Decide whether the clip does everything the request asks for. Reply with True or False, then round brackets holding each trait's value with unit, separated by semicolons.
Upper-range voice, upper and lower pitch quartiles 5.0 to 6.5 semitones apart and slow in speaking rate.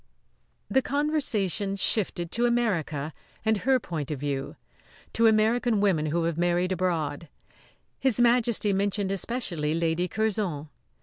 True (195 Hz; 5.6 semitones; 125 wpm)